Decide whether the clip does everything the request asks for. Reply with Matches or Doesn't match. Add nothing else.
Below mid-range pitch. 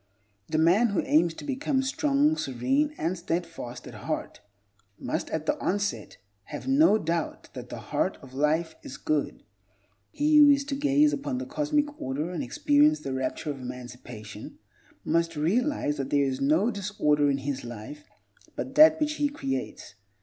Doesn't match